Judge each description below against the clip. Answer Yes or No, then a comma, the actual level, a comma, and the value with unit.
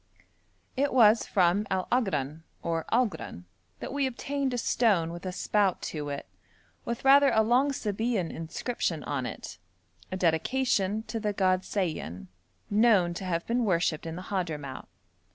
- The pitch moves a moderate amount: No, wide, 6.0 semitones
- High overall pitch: Yes, high, 195 Hz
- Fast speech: No, average, 155 wpm